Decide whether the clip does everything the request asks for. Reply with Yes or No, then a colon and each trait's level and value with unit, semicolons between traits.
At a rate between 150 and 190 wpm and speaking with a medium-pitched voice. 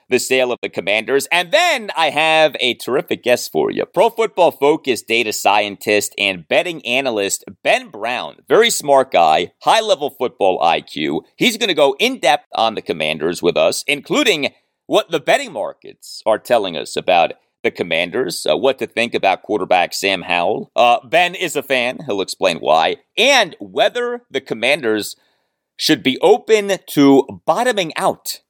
Yes: average, 165 wpm; medium, 155 Hz